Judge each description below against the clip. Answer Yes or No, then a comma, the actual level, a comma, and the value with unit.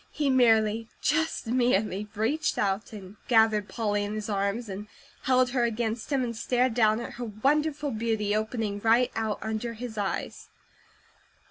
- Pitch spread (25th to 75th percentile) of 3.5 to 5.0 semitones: No, average, 2.7 semitones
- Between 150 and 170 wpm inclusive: Yes, average, 155 wpm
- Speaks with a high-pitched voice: Yes, high, 225 Hz